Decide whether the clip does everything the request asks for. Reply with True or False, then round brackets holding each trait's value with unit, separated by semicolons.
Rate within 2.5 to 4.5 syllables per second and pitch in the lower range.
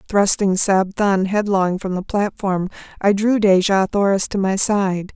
False (4.2 syllables/s; 195 Hz)